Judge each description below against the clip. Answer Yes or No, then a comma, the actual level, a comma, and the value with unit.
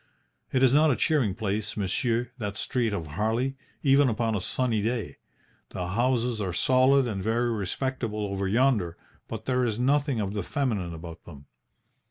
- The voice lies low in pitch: Yes, low, 115 Hz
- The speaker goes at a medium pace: Yes, average, 170 wpm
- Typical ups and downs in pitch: Yes, average, 4.4 semitones